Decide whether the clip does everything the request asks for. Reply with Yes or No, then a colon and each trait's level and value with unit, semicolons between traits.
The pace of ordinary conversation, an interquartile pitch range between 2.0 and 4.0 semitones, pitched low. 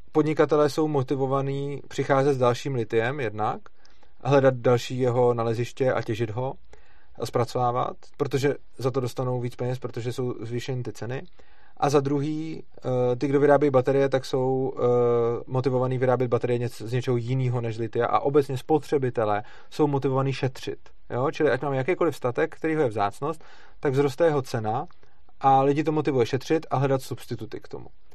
Yes: average, 160 wpm; narrow, 2.5 semitones; low, 130 Hz